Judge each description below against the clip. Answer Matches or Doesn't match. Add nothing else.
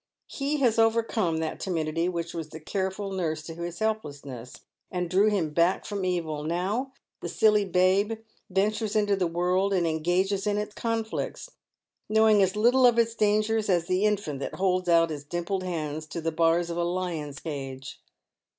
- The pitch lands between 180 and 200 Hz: Matches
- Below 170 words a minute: Doesn't match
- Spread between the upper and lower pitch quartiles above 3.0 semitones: Matches